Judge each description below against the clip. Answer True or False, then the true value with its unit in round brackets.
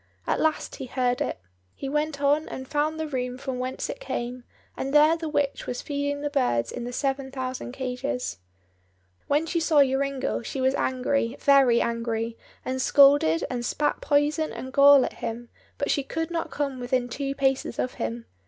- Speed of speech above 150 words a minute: True (185 wpm)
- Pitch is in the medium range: False (270 Hz)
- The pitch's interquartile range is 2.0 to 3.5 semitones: True (2.6 semitones)